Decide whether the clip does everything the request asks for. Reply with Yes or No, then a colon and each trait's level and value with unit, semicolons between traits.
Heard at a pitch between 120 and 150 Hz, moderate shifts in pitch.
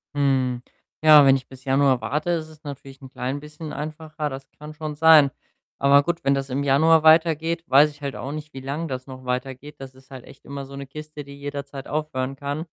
No: medium, 140 Hz; narrow, 2.3 semitones